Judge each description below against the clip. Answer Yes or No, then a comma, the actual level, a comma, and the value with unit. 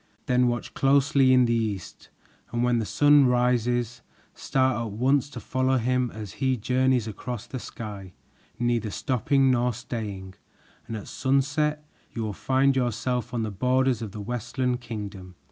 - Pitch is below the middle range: Yes, low, 125 Hz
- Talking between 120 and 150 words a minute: No, average, 160 wpm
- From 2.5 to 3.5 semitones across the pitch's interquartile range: Yes, average, 2.8 semitones